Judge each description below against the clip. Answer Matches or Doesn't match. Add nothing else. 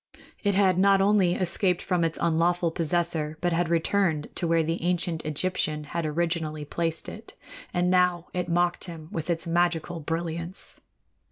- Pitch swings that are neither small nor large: Doesn't match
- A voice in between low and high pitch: Matches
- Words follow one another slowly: Doesn't match